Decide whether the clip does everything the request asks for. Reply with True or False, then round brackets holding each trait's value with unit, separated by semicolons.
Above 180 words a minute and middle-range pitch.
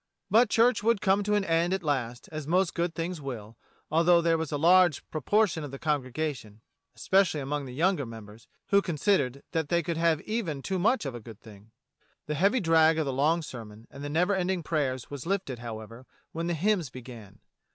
True (205 wpm; 155 Hz)